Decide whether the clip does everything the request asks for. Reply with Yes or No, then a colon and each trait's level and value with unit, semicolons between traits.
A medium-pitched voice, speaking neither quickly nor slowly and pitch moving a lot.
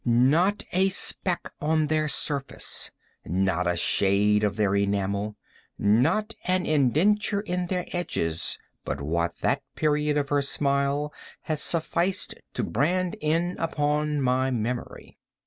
No: medium, 145 Hz; slow, 115 wpm; wide, 8.3 semitones